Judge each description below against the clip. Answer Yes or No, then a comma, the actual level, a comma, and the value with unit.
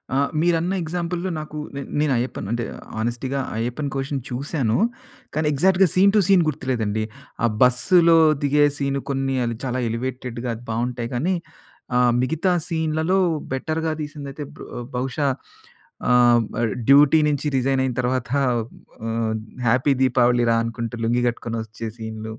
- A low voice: Yes, low, 130 Hz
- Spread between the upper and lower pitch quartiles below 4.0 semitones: No, average, 4.3 semitones